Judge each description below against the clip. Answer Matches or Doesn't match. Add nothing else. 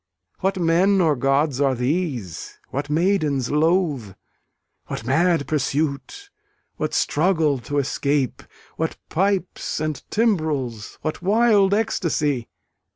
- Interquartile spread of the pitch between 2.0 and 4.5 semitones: Doesn't match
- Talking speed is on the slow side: Matches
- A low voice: Doesn't match